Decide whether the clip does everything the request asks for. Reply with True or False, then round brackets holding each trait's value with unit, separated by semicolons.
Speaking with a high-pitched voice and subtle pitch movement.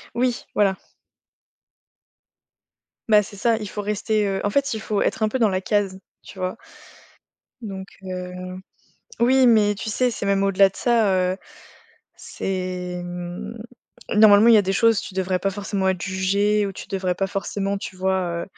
True (200 Hz; 2.2 semitones)